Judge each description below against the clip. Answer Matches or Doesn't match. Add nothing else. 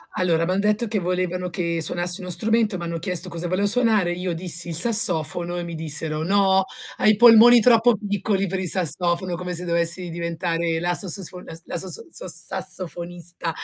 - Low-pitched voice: Doesn't match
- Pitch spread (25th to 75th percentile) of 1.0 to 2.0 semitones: Doesn't match